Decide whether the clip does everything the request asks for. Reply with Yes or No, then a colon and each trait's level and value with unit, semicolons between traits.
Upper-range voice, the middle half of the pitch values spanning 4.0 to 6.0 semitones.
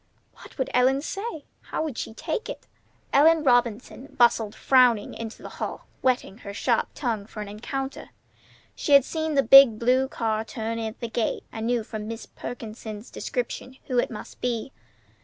No: high, 240 Hz; average, 3.4 semitones